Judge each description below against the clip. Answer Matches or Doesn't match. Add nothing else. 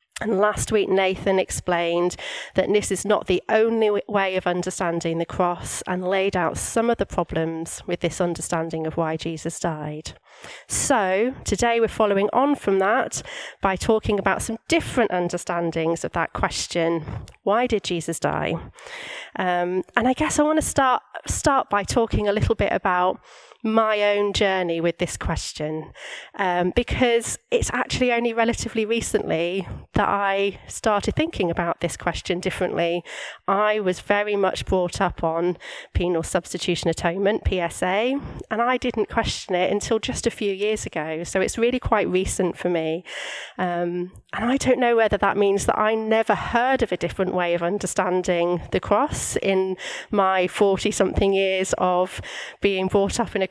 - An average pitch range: Matches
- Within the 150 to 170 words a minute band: Matches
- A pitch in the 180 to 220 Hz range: Matches